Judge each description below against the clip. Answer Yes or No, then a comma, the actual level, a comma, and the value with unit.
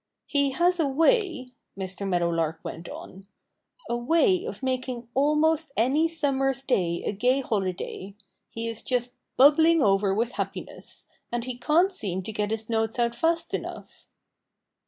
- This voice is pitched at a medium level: No, very high, 250 Hz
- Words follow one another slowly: No, average, 150 wpm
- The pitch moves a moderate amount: No, wide, 6.5 semitones